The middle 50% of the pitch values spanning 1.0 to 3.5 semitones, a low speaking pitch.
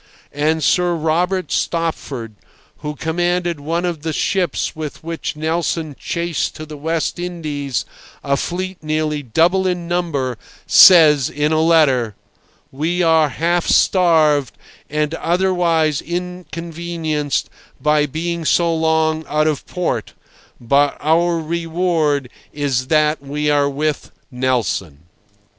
No: narrow, 2.6 semitones; medium, 160 Hz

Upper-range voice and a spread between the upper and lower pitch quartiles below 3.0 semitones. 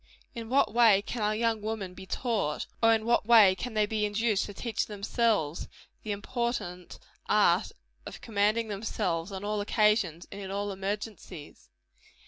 Yes: high, 210 Hz; narrow, 2.5 semitones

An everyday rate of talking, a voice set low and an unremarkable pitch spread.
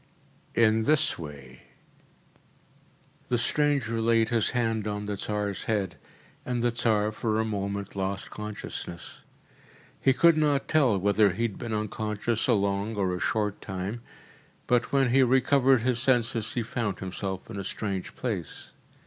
Yes: average, 150 wpm; low, 110 Hz; average, 3.4 semitones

